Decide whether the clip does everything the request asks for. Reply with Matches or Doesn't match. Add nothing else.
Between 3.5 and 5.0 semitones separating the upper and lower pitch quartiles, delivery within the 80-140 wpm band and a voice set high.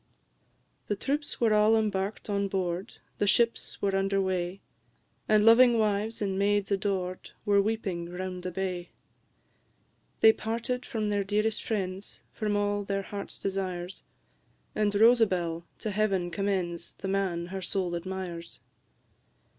Doesn't match